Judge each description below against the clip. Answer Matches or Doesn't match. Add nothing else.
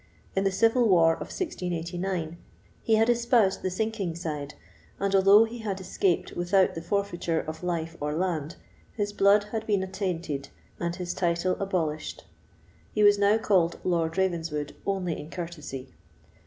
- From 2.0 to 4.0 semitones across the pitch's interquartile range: Matches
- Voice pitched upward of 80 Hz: Matches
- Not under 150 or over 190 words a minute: Matches